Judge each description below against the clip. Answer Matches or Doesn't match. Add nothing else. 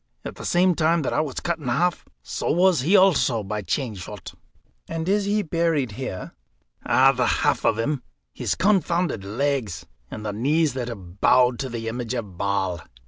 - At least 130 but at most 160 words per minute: Doesn't match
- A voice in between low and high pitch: Doesn't match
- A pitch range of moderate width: Doesn't match